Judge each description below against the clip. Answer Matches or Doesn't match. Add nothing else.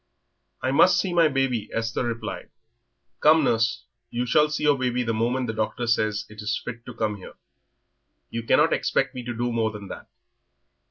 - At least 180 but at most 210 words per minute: Matches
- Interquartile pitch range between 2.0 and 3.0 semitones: Matches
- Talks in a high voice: Doesn't match